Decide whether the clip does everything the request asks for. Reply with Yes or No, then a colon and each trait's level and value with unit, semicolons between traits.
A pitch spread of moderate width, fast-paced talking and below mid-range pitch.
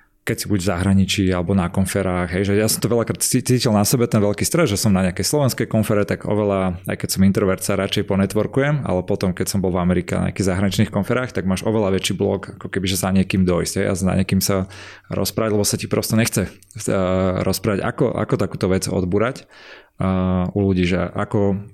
No: narrow, 2.3 semitones; fast, 220 wpm; low, 100 Hz